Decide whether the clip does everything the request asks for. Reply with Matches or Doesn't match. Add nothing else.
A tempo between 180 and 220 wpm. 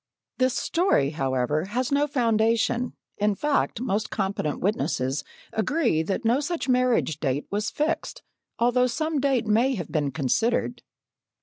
Doesn't match